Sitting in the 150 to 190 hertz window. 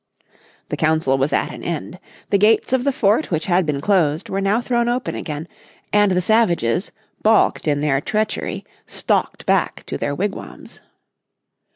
Yes: medium, 185 Hz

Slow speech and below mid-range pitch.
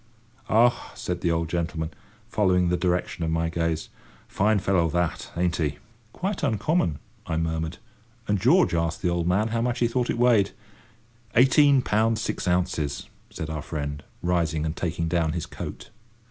No: average, 165 wpm; very low, 90 Hz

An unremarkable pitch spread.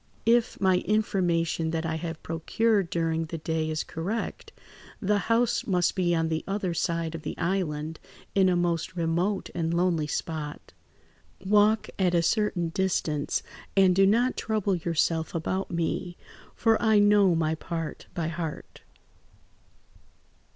Yes: average, 3.2 semitones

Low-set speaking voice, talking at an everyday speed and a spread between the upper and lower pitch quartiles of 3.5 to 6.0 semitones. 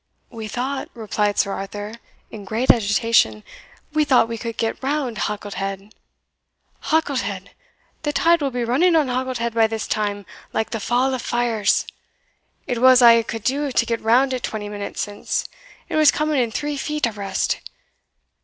No: high, 230 Hz; average, 175 wpm; average, 4.0 semitones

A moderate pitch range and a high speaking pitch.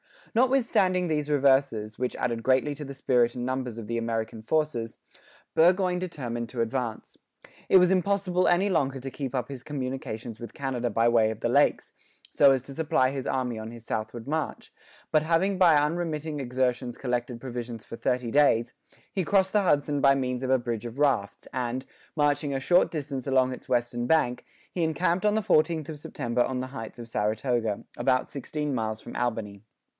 No: average, 4.4 semitones; low, 130 Hz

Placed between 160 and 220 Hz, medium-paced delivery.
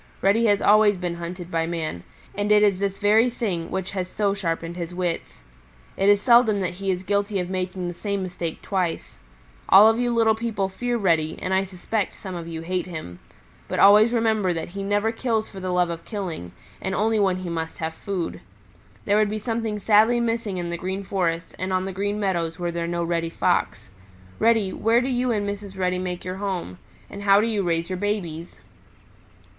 No: high, 190 Hz; fast, 210 wpm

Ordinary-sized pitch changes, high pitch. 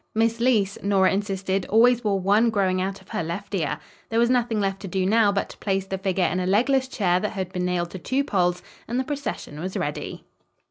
Yes: average, 3.3 semitones; high, 195 Hz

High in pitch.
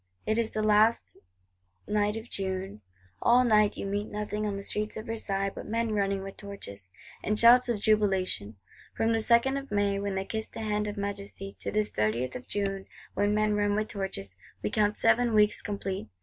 Yes: high, 210 Hz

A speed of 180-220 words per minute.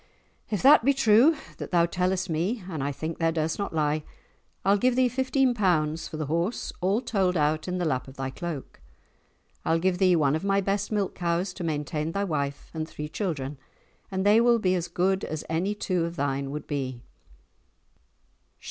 Yes: average, 195 wpm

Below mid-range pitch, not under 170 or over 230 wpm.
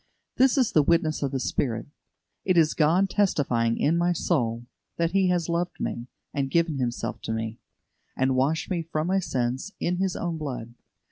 No: medium, 155 Hz; average, 185 wpm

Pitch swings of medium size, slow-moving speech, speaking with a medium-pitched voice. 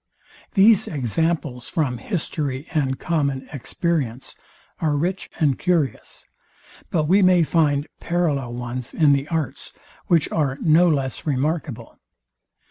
Yes: average, 4.0 semitones; slow, 120 wpm; medium, 150 Hz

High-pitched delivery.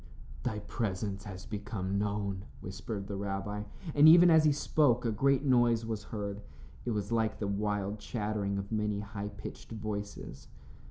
No: low, 105 Hz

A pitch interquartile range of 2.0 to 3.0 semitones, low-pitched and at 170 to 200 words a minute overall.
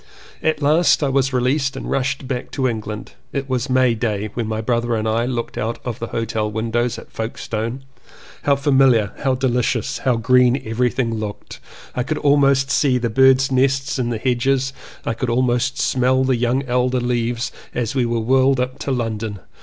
Yes: narrow, 2.4 semitones; low, 125 Hz; average, 180 wpm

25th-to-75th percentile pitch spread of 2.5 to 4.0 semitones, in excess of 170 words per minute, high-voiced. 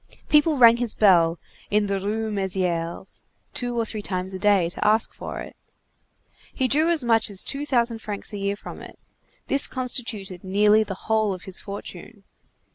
Yes: average, 3.5 semitones; average, 180 wpm; high, 210 Hz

